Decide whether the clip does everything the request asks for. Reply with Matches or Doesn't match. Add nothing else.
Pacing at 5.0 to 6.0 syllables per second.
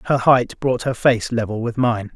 Doesn't match